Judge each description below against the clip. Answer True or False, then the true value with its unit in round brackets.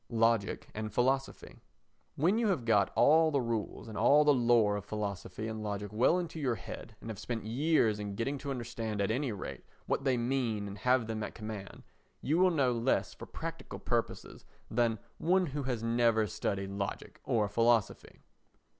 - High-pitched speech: False (115 Hz)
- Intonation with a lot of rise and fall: False (4.1 semitones)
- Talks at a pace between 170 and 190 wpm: True (180 wpm)